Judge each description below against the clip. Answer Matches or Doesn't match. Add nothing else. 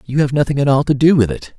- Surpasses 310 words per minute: Matches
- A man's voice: Matches